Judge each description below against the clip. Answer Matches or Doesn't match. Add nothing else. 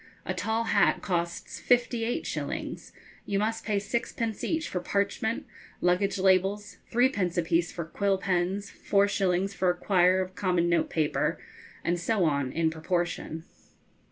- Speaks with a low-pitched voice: Doesn't match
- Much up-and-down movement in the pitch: Doesn't match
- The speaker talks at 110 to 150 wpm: Matches